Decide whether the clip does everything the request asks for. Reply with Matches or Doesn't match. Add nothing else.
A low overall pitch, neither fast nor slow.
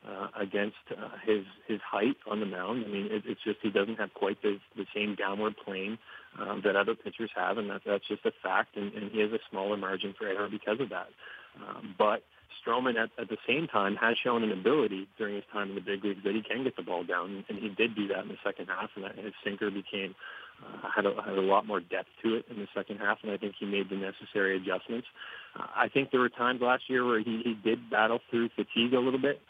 Doesn't match